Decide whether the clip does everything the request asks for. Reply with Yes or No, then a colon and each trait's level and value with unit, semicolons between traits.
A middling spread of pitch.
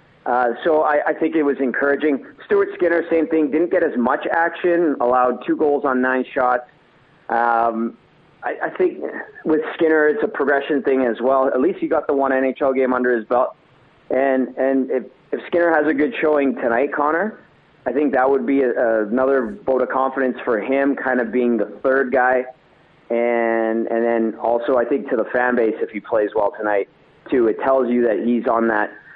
Yes: average, 3.6 semitones